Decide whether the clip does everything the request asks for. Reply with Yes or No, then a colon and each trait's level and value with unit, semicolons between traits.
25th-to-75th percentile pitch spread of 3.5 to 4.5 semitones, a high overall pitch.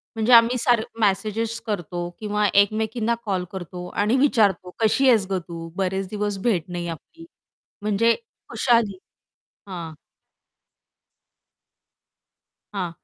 Yes: average, 3.9 semitones; high, 205 Hz